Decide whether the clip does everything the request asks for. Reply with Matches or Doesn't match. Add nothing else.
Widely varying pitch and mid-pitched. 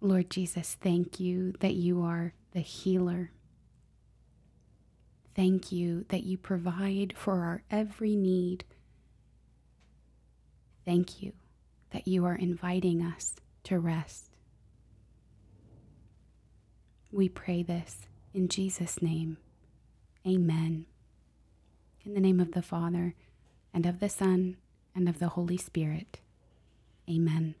Matches